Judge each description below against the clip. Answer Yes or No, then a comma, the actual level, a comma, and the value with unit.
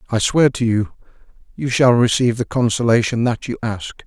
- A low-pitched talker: Yes, low, 120 Hz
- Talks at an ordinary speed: Yes, average, 175 wpm